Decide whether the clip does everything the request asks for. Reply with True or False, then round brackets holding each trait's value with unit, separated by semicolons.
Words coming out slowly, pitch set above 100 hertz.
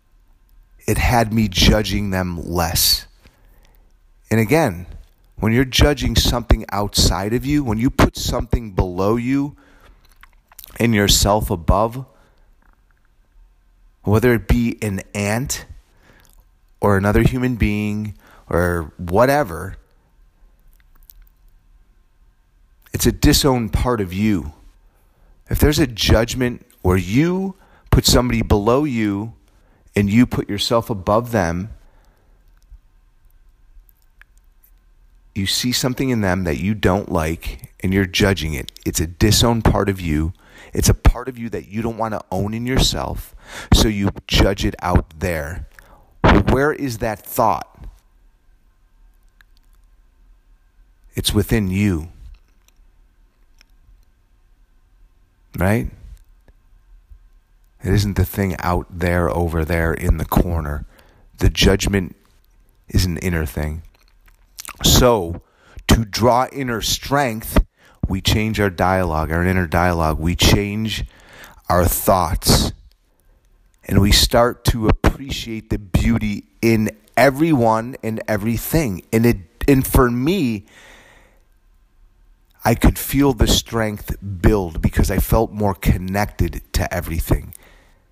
False (110 wpm; 95 Hz)